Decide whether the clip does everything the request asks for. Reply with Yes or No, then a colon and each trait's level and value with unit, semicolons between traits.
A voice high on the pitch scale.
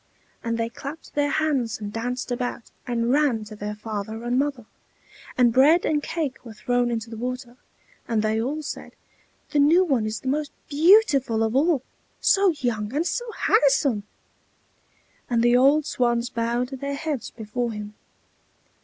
Yes: high, 245 Hz